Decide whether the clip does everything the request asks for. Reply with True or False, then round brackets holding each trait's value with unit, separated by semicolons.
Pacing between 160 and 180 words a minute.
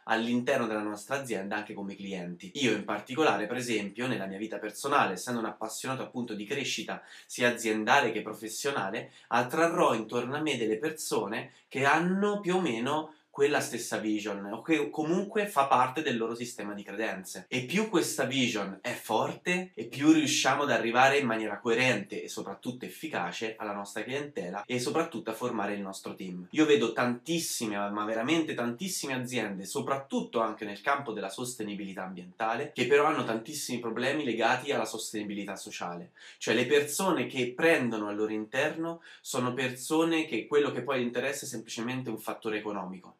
True (165 wpm)